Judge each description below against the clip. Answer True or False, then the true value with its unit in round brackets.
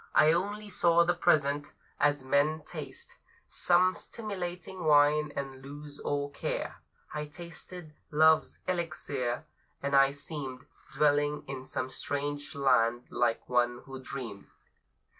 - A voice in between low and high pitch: True (145 Hz)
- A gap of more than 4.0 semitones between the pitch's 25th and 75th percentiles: False (3.2 semitones)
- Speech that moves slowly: True (120 wpm)